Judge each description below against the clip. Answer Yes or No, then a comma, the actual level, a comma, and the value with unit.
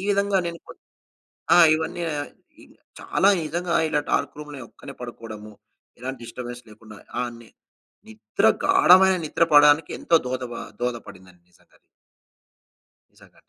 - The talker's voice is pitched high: No, low, 130 Hz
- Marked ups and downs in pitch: Yes, wide, 6.2 semitones